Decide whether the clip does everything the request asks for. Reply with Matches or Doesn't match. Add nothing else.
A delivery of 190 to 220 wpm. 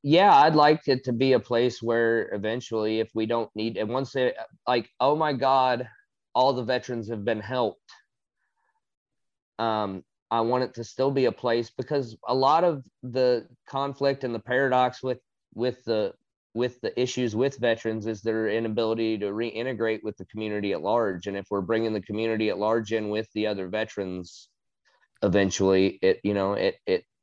Doesn't match